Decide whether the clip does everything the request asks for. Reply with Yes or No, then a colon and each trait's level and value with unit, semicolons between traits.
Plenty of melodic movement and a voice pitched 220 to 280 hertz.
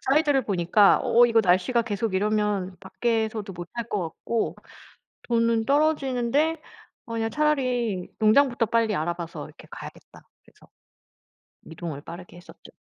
No: average, 4.5 semitones; high, 225 Hz